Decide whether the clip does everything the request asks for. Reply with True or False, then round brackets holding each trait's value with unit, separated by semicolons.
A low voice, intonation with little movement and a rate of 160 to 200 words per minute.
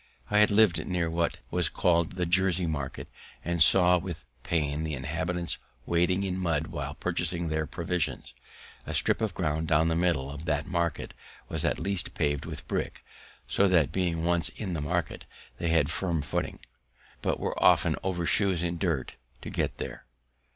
True (85 Hz; 2.3 semitones; 175 wpm)